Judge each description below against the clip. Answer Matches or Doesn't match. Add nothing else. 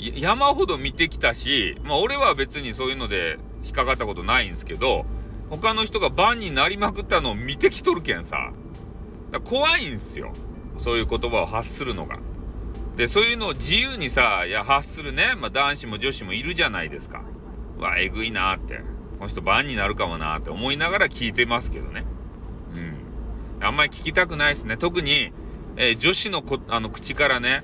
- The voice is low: Matches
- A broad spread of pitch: Matches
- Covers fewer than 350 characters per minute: Doesn't match